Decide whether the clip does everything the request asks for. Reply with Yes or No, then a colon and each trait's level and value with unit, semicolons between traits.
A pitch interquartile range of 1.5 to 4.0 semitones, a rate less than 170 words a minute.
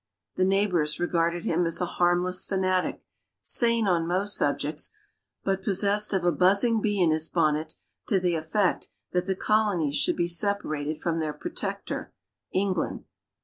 Yes: average, 3.2 semitones; average, 150 wpm